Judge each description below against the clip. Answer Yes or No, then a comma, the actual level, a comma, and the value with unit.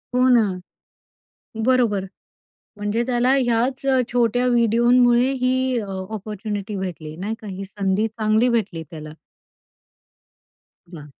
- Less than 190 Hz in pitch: No, high, 225 Hz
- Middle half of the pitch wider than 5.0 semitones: No, average, 3.6 semitones